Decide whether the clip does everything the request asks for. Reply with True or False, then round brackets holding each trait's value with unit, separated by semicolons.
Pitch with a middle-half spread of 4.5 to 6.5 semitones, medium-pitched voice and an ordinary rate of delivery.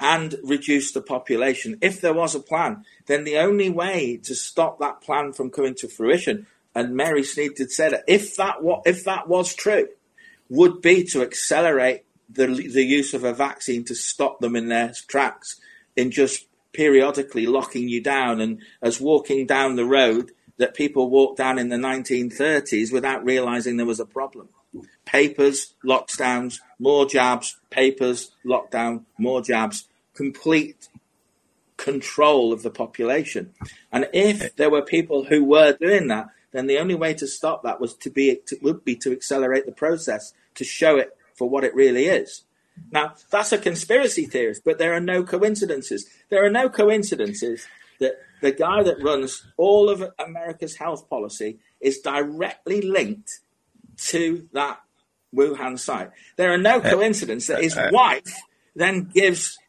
True (5.5 semitones; 145 Hz; 165 wpm)